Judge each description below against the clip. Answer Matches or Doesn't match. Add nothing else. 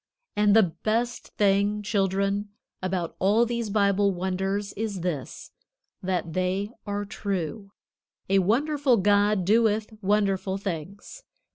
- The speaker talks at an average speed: Doesn't match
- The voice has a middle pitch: Doesn't match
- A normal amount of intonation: Doesn't match